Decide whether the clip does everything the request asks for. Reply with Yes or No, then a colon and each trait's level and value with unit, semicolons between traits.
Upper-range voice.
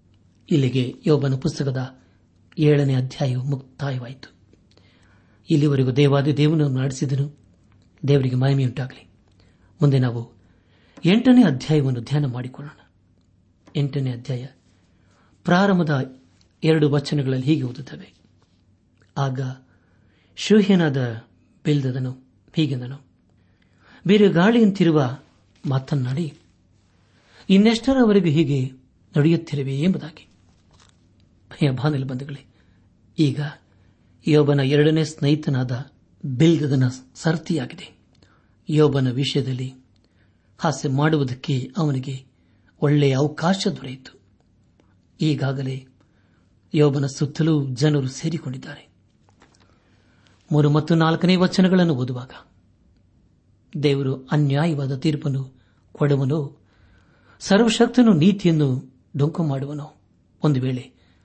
No: low, 135 Hz